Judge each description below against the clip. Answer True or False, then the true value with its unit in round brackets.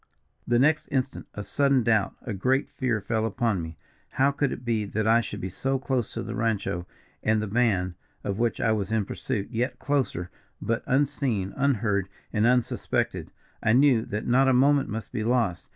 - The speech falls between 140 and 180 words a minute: False (190 wpm)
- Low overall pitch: True (115 Hz)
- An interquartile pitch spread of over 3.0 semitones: True (4.0 semitones)